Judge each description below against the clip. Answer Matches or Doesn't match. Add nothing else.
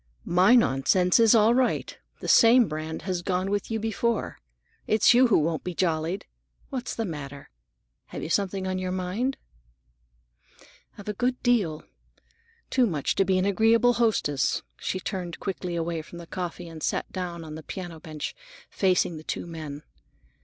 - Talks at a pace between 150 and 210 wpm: Matches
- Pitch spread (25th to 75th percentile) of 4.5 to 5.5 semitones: Matches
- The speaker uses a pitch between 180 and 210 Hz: Matches